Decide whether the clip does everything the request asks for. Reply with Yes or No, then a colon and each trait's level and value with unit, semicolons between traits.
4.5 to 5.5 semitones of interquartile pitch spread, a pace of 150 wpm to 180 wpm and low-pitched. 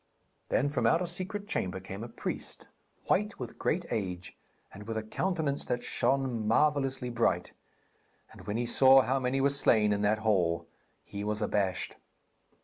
Yes: average, 5.1 semitones; average, 165 wpm; low, 120 Hz